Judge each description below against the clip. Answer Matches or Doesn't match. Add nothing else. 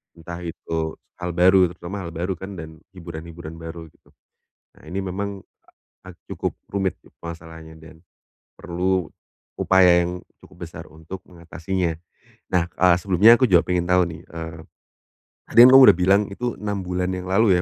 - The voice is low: Matches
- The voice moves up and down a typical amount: Doesn't match